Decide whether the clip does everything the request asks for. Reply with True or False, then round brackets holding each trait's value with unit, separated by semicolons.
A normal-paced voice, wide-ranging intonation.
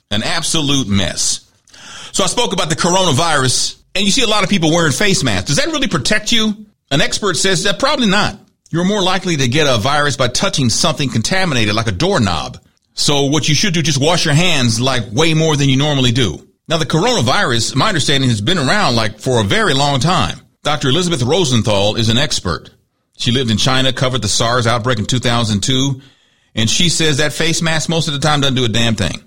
False (215 wpm; 5.8 semitones)